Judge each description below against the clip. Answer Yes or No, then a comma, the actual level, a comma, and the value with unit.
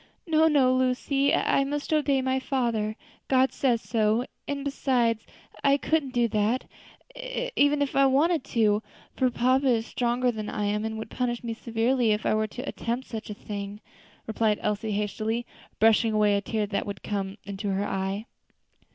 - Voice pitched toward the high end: Yes, high, 235 Hz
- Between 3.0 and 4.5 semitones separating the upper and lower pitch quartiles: Yes, average, 3.9 semitones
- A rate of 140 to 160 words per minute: No, average, 170 wpm